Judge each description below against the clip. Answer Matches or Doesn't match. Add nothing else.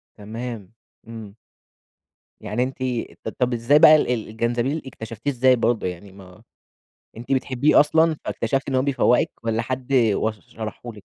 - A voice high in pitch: Doesn't match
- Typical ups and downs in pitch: Matches